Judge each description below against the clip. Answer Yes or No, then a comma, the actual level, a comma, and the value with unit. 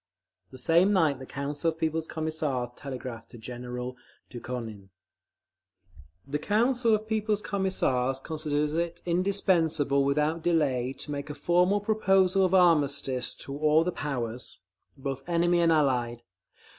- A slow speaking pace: Yes, slow, 130 wpm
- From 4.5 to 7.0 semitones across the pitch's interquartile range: Yes, average, 5.0 semitones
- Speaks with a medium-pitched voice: Yes, medium, 150 Hz